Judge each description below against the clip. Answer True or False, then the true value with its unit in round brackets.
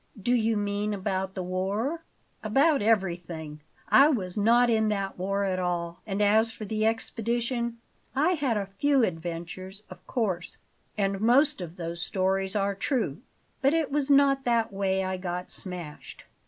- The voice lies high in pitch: True (205 Hz)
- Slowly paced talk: False (160 wpm)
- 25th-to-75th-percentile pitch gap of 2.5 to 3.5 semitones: False (4.2 semitones)